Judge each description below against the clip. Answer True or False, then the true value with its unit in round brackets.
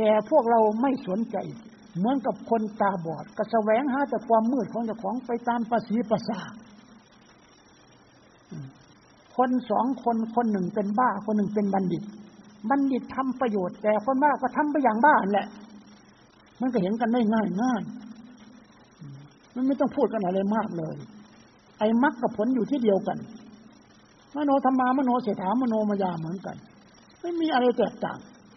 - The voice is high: True (225 Hz)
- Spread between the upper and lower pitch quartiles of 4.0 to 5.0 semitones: False (3.2 semitones)